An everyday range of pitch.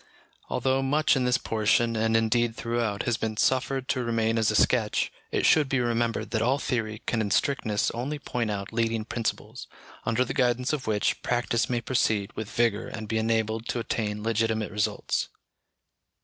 No: narrow, 2.0 semitones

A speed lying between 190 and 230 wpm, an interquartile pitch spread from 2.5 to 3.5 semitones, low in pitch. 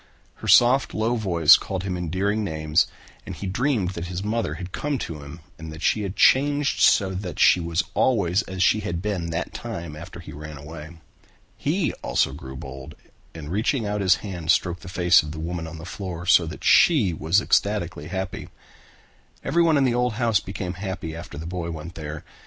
No: average, 200 wpm; average, 4.3 semitones; very low, 90 Hz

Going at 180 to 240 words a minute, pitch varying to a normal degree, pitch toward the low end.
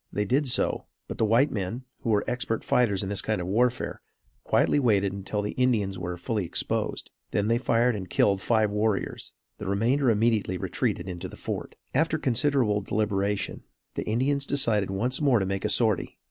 Yes: average, 185 wpm; average, 3.9 semitones; low, 110 Hz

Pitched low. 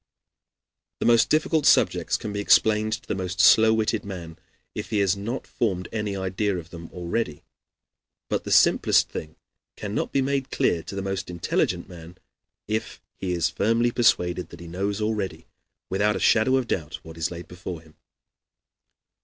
Yes: low, 100 Hz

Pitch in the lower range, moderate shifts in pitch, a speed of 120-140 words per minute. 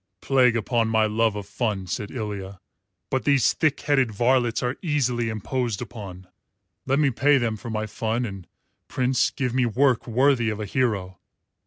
No: low, 115 Hz; average, 3.3 semitones; average, 170 wpm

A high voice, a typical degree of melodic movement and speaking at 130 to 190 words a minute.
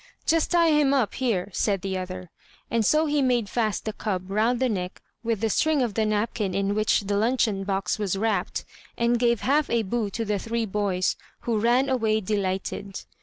No: high, 220 Hz; average, 3.5 semitones; average, 200 wpm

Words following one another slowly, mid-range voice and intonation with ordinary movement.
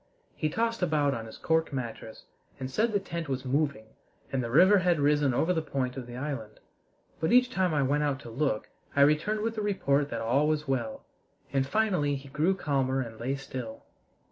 No: fast, 205 wpm; medium, 145 Hz; average, 4.3 semitones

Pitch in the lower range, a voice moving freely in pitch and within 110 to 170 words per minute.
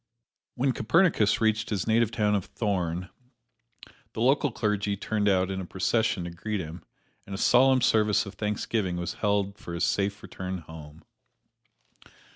No: low, 105 Hz; average, 3.2 semitones; average, 155 wpm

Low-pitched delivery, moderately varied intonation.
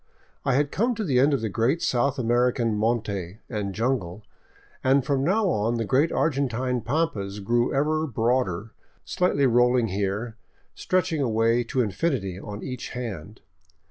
Yes: low, 120 Hz; average, 4.3 semitones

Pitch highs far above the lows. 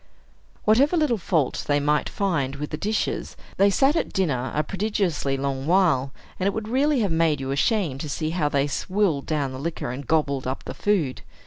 Yes: wide, 6.4 semitones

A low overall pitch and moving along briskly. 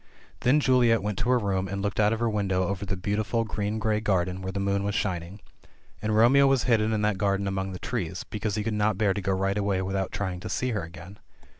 Yes: low, 100 Hz; fast, 255 wpm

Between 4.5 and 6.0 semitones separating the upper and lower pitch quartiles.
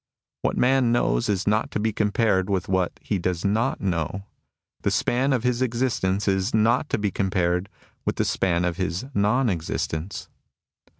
No: average, 4.0 semitones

